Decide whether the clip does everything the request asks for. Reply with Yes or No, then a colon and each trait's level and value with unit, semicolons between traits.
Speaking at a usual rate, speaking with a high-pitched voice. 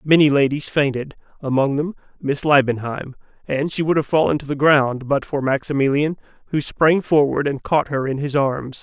No: average, 175 wpm; medium, 140 Hz